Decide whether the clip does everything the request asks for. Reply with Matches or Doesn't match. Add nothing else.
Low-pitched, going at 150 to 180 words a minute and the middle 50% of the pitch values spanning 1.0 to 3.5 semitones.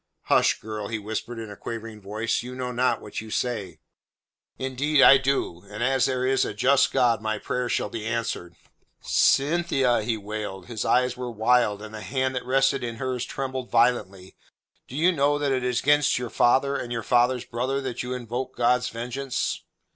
Doesn't match